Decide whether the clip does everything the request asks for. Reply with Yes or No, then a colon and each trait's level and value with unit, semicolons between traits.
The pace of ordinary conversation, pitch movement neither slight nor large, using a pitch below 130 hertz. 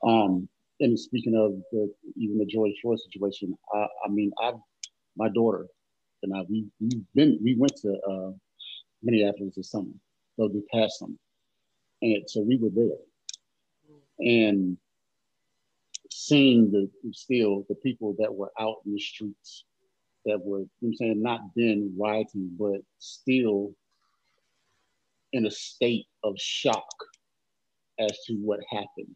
No: average, 145 wpm; narrow, 2.2 semitones; low, 105 Hz